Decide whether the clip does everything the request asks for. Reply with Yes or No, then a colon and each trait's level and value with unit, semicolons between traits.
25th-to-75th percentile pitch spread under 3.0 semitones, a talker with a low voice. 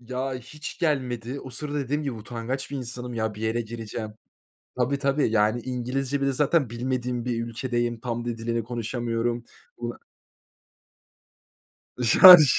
Yes: narrow, 2.5 semitones; low, 120 Hz